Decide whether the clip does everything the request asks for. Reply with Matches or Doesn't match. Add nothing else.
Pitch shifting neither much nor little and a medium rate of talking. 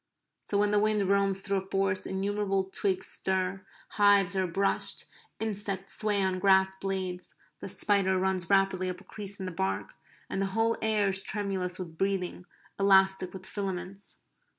Doesn't match